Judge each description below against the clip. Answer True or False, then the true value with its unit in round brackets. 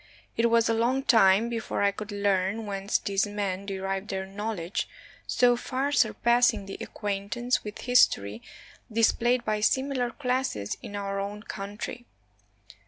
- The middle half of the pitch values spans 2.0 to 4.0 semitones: True (3.3 semitones)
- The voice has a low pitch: False (210 Hz)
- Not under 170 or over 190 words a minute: False (145 wpm)